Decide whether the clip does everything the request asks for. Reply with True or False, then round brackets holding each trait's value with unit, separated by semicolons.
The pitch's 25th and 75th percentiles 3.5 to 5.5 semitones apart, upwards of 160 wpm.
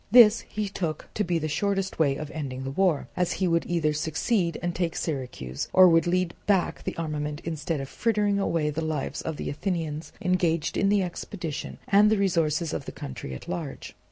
True (3.9 semitones; 200 wpm)